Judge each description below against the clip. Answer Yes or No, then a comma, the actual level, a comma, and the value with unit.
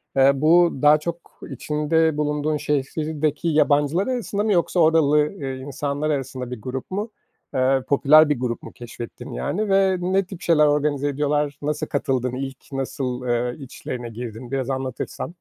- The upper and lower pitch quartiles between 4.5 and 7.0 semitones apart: No, average, 3.2 semitones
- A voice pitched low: No, medium, 145 Hz